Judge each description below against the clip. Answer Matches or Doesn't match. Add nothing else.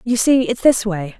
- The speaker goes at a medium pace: Doesn't match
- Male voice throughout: Doesn't match